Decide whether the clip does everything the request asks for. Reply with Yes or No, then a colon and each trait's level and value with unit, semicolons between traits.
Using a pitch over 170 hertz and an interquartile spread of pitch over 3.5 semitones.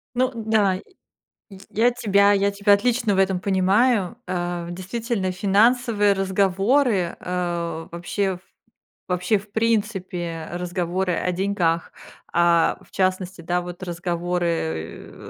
No: high, 190 Hz; average, 2.8 semitones